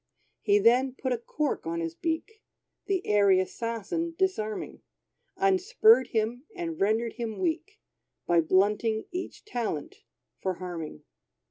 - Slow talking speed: Yes, slow, 125 wpm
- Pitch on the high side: Yes, high, 235 Hz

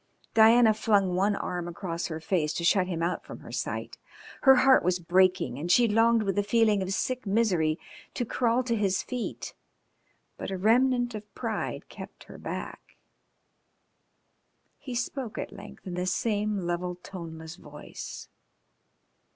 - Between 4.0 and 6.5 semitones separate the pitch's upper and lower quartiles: Yes, average, 4.6 semitones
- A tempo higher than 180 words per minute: No, average, 155 wpm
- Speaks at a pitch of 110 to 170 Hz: No, high, 200 Hz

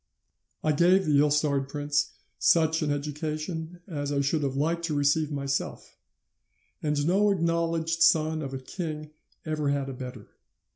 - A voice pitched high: No, medium, 150 Hz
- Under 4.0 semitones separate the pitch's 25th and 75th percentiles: Yes, narrow, 2.4 semitones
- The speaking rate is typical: Yes, average, 155 wpm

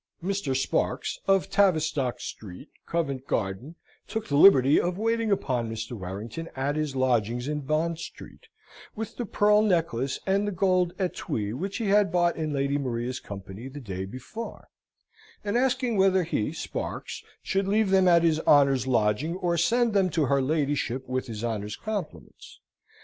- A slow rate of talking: No, average, 160 wpm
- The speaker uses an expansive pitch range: Yes, wide, 7.1 semitones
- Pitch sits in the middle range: Yes, medium, 155 Hz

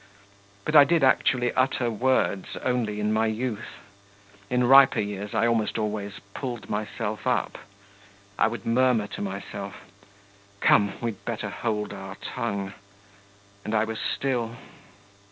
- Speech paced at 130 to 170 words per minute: Yes, slow, 135 wpm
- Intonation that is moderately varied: Yes, average, 3.2 semitones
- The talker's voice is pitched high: No, low, 110 Hz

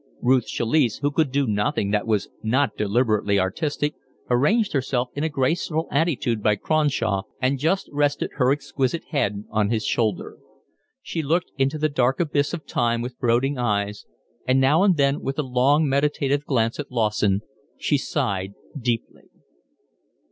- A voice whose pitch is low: Yes, low, 130 Hz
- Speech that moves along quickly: No, average, 155 wpm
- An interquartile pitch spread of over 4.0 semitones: Yes, average, 4.4 semitones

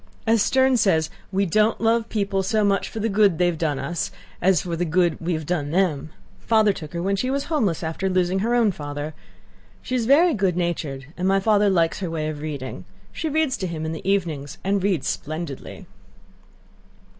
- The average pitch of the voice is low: No, medium, 185 Hz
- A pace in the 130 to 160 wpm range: No, fast, 205 wpm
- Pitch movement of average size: Yes, average, 4.9 semitones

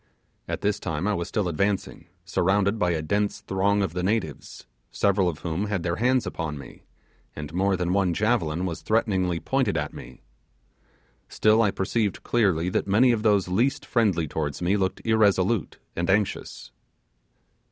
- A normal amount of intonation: Yes, average, 3.5 semitones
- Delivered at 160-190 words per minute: Yes, average, 165 wpm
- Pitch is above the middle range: No, very low, 95 Hz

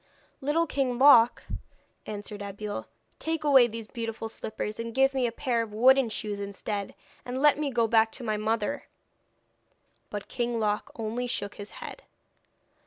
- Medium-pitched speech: No, high, 230 Hz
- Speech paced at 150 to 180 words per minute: Yes, average, 160 wpm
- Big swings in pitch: No, average, 3.5 semitones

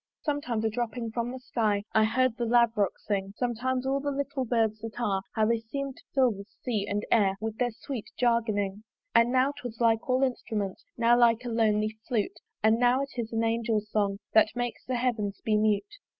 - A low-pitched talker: No, high, 230 Hz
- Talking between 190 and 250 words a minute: Yes, average, 200 wpm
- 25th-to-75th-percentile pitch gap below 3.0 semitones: Yes, narrow, 2.4 semitones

